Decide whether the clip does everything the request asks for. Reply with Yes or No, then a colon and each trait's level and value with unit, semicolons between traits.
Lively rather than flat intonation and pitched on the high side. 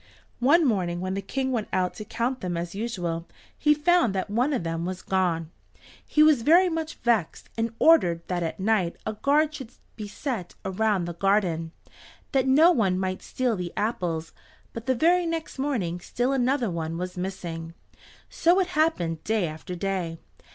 Yes: wide, 7.3 semitones; high, 210 Hz